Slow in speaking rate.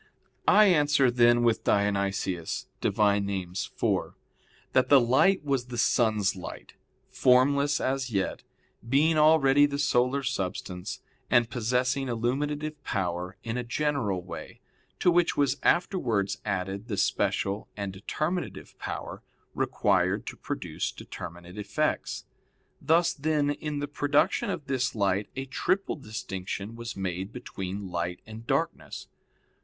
Yes: slow, 130 wpm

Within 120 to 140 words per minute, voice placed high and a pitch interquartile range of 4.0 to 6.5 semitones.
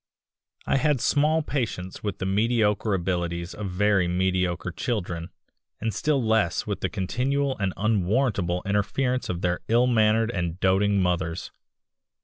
No: slow, 135 wpm; low, 100 Hz; average, 4.3 semitones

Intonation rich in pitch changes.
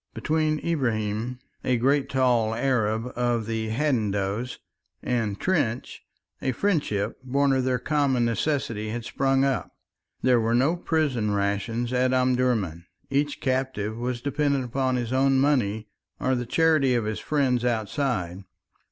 No: average, 3.4 semitones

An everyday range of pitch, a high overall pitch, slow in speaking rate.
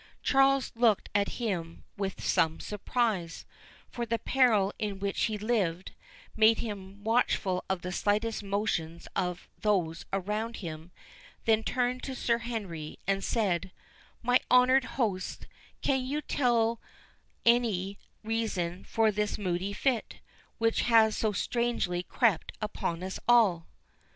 Yes: average, 3.9 semitones; high, 210 Hz; slow, 125 wpm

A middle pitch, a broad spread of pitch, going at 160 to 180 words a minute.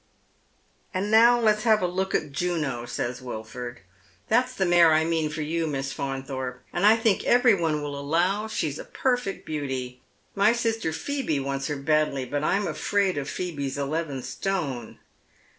Yes: medium, 160 Hz; wide, 6.4 semitones; average, 175 wpm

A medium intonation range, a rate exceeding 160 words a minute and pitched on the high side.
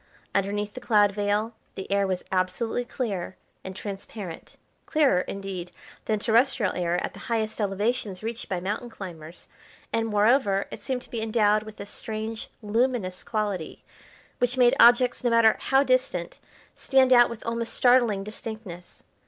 No: average, 3.4 semitones; average, 155 wpm; high, 215 Hz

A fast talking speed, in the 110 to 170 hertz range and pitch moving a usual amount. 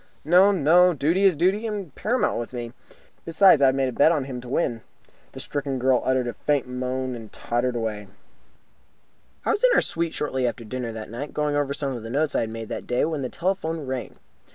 Yes: fast, 220 wpm; low, 135 Hz; average, 4.9 semitones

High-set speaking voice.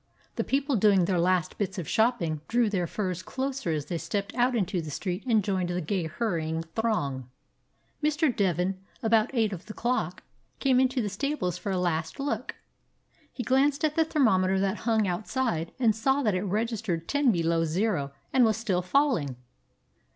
Yes: high, 205 Hz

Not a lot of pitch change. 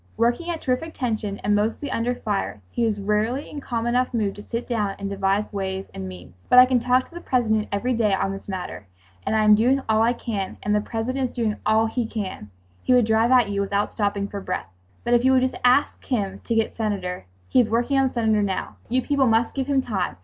No: average, 3.7 semitones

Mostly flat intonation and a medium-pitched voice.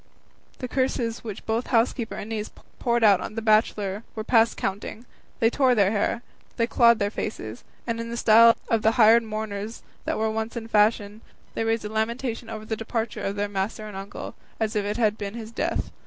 No: narrow, 1.6 semitones; high, 220 Hz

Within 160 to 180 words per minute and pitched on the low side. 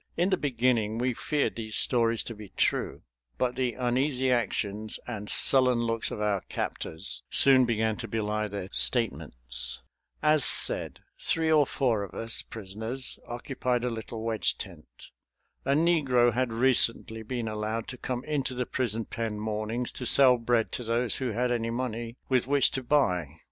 Yes: average, 165 wpm; low, 120 Hz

